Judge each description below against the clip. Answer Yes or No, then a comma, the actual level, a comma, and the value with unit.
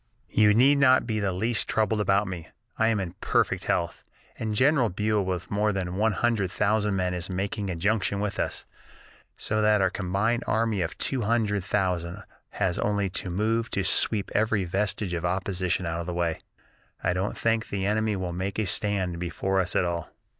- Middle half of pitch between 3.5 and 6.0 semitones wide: No, average, 3.0 semitones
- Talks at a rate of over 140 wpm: Yes, average, 195 wpm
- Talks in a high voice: No, low, 100 Hz